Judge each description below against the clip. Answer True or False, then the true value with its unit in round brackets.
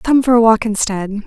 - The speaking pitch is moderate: False (220 Hz)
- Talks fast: True (235 wpm)